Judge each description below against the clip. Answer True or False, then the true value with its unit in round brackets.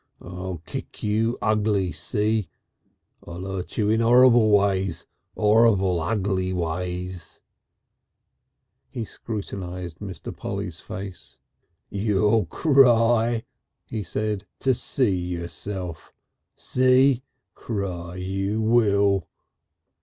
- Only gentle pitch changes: False (3.5 semitones)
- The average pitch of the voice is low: True (100 Hz)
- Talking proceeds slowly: True (90 wpm)